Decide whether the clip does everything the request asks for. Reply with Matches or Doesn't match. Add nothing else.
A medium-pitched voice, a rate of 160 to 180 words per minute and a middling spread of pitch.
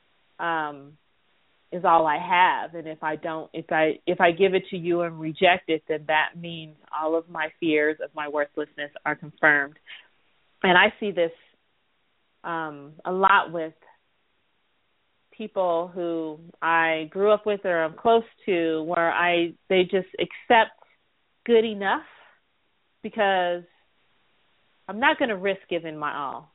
Doesn't match